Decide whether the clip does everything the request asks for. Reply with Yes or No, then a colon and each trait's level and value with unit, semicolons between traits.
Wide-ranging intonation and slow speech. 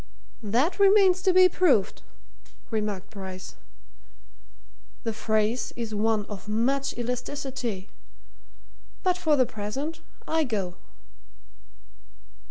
Yes: wide, 6.6 semitones; slow, 95 wpm